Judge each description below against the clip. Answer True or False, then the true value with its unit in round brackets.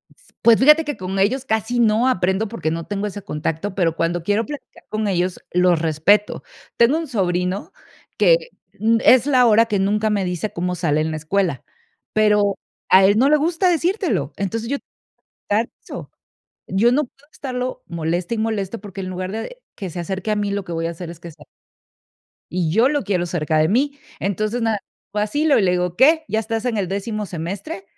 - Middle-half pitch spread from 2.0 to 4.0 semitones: False (4.6 semitones)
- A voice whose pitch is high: True (205 Hz)